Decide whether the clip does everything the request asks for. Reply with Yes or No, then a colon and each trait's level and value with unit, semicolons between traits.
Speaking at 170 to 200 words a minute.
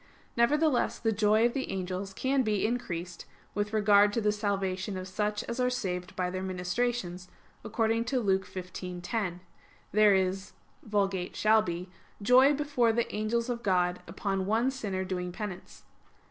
No: average, 150 wpm